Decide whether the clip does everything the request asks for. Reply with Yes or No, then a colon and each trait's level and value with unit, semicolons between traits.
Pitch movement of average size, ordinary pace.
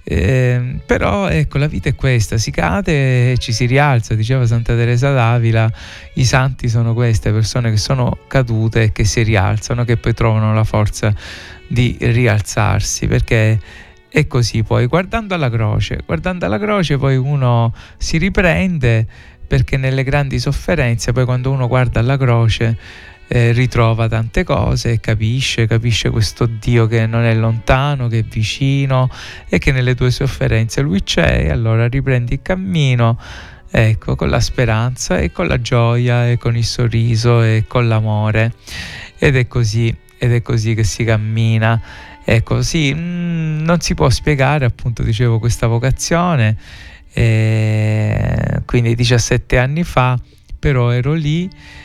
Yes: average, 3.0 semitones; average, 150 wpm